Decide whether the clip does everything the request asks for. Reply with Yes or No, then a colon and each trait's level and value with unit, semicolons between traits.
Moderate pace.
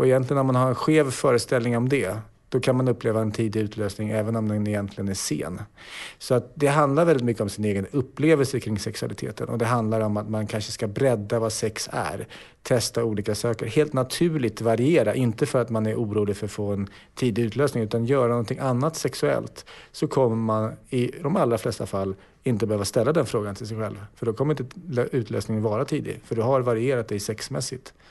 No: fast, 210 wpm